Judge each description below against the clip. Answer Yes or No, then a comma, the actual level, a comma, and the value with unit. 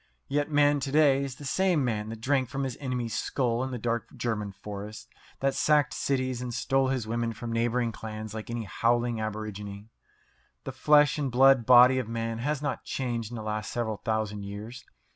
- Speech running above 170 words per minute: Yes, average, 195 wpm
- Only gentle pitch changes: No, average, 3.5 semitones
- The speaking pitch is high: No, low, 120 Hz